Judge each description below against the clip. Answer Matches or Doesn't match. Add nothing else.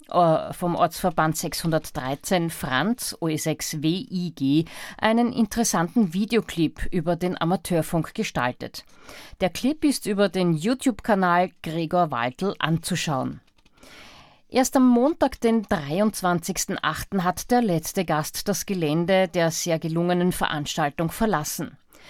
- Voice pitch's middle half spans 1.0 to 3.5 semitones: Doesn't match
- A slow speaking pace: Matches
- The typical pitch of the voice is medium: Matches